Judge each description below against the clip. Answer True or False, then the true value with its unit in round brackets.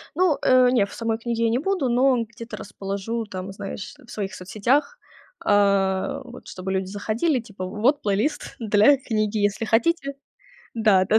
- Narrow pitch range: False (4.0 semitones)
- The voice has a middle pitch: False (225 Hz)